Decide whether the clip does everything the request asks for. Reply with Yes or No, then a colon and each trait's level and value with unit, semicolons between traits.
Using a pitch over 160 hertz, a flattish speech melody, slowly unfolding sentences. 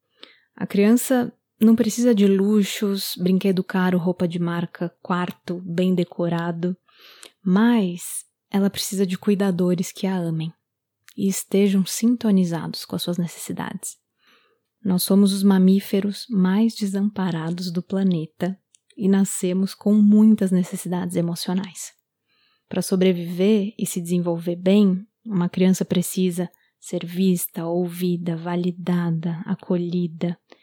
Yes: medium, 185 Hz; narrow, 2.1 semitones; slow, 110 wpm